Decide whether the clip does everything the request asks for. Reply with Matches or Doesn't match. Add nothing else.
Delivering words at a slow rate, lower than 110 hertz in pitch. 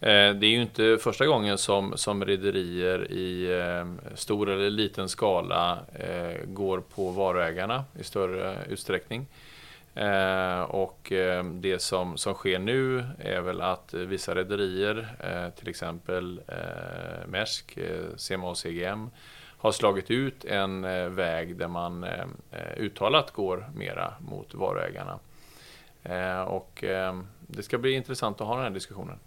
Matches